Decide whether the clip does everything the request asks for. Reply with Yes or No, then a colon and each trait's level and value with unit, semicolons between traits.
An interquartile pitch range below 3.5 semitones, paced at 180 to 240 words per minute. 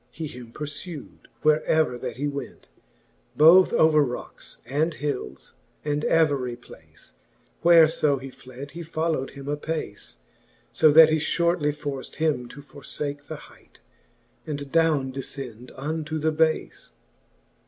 No: narrow, 2.5 semitones; average, 140 wpm